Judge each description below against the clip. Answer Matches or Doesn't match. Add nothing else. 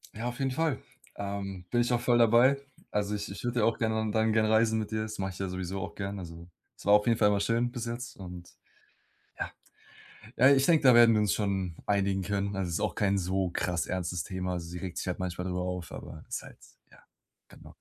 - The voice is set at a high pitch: Doesn't match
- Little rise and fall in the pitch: Doesn't match